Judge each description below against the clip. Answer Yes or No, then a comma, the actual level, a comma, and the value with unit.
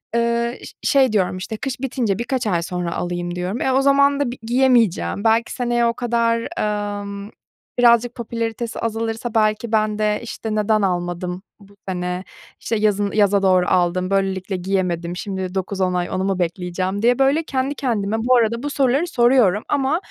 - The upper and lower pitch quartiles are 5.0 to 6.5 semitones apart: No, average, 4.3 semitones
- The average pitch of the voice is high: Yes, high, 215 Hz